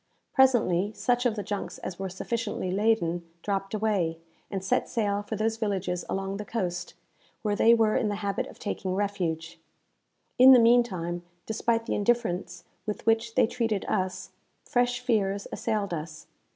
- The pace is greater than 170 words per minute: No, average, 160 wpm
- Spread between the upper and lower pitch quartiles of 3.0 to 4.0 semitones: Yes, average, 3.5 semitones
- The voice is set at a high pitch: Yes, high, 205 Hz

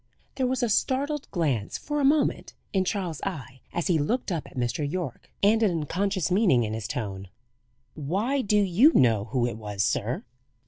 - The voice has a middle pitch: Yes, medium, 175 Hz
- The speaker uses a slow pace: No, average, 185 wpm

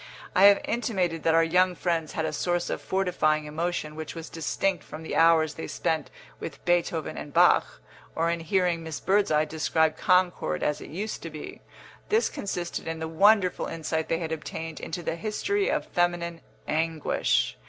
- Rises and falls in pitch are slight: Yes, narrow, 2.1 semitones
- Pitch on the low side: No, medium, 165 Hz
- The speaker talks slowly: No, average, 175 wpm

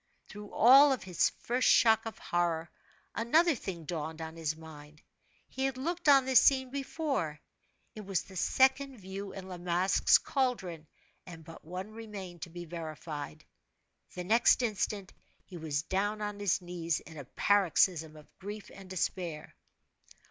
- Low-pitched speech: No, high, 190 Hz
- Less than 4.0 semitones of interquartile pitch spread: No, wide, 5.5 semitones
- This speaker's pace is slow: No, average, 155 wpm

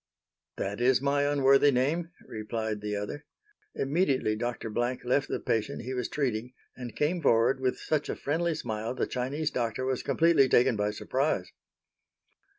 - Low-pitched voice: Yes, low, 130 Hz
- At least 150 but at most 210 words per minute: Yes, average, 155 wpm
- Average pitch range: Yes, average, 3.9 semitones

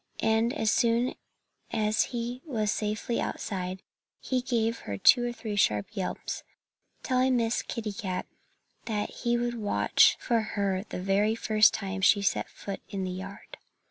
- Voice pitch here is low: No, high, 220 Hz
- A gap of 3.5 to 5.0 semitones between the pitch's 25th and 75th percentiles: No, average, 3.1 semitones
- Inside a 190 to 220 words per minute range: No, average, 150 wpm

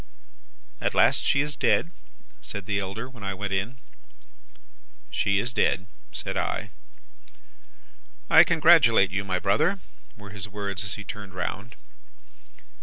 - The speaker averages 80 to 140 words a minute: Yes, slow, 135 wpm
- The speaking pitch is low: Yes, low, 100 Hz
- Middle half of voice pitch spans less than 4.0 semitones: Yes, average, 3.5 semitones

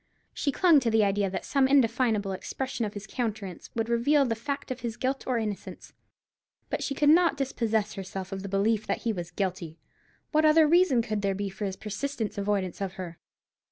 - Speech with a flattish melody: No, average, 5.1 semitones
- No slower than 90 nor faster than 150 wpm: No, average, 200 wpm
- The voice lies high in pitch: Yes, high, 220 Hz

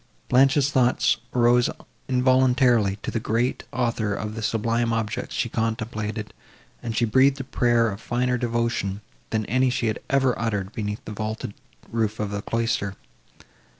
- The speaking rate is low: No, average, 150 wpm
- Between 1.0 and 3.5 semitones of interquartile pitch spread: Yes, narrow, 2.5 semitones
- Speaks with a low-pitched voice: Yes, low, 115 Hz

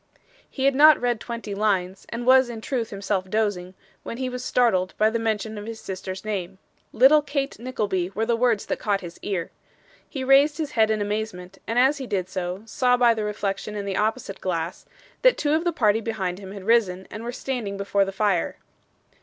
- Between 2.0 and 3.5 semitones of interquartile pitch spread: No, average, 4.1 semitones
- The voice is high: Yes, high, 215 Hz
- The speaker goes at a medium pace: No, fast, 210 wpm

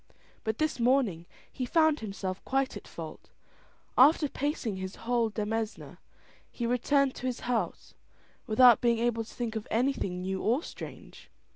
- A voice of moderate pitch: No, high, 235 Hz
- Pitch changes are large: No, average, 3.3 semitones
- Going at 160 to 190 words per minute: No, average, 150 wpm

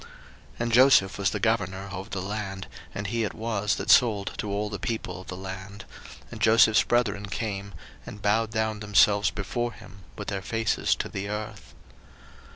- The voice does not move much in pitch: Yes, narrow, 2.2 semitones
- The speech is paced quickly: No, average, 180 wpm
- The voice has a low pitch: Yes, low, 105 Hz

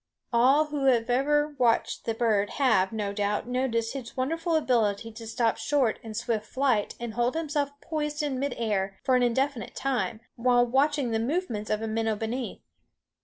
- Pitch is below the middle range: No, high, 245 Hz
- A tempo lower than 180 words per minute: Yes, average, 170 wpm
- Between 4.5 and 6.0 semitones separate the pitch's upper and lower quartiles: No, average, 3.8 semitones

